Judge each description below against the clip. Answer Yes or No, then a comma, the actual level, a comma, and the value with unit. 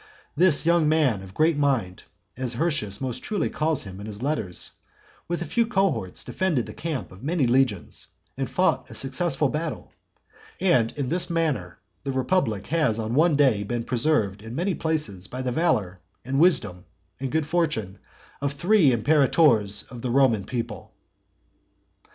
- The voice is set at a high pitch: No, low, 130 Hz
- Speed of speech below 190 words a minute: Yes, average, 165 wpm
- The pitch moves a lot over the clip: Yes, wide, 6.6 semitones